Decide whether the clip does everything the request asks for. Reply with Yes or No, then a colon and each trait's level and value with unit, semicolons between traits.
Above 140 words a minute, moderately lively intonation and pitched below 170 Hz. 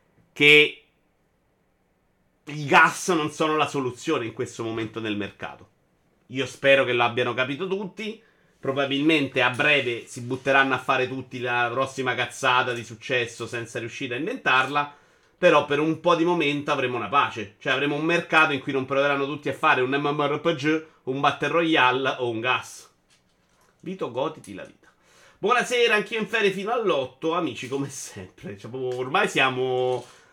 Yes: average, 155 wpm; average, 3.5 semitones; medium, 140 Hz